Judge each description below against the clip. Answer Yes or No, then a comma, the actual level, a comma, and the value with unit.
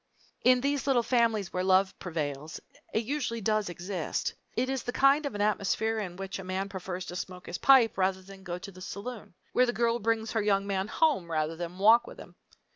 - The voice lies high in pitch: Yes, high, 200 Hz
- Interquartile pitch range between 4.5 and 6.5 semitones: No, average, 4.1 semitones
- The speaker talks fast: Yes, fast, 215 wpm